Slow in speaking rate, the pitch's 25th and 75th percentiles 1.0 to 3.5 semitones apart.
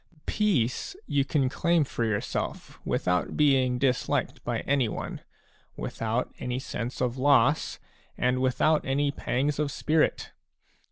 Yes: slow, 120 wpm; average, 2.8 semitones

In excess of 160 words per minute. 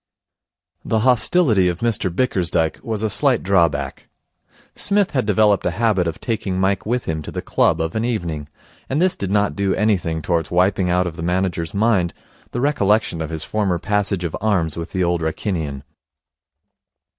Yes: average, 175 wpm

